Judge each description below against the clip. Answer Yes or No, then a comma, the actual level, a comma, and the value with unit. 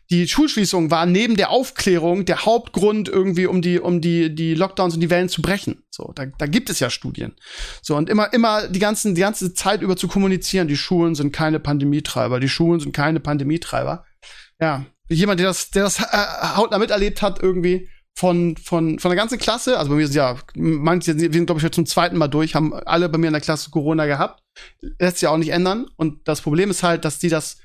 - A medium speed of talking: No, fast, 220 wpm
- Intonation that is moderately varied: Yes, average, 3.3 semitones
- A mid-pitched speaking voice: Yes, medium, 175 Hz